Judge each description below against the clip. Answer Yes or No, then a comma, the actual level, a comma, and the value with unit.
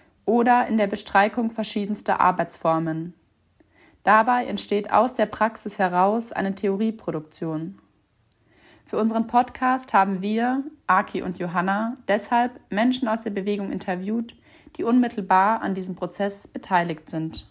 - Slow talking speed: Yes, slow, 120 wpm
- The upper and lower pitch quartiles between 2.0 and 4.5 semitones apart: Yes, average, 3.5 semitones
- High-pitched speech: Yes, high, 205 Hz